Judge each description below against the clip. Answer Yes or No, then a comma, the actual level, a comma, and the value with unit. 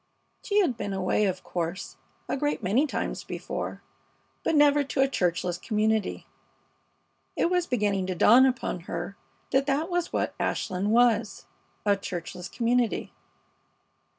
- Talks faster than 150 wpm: No, average, 140 wpm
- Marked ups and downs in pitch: Yes, wide, 6.4 semitones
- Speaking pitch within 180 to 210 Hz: No, high, 220 Hz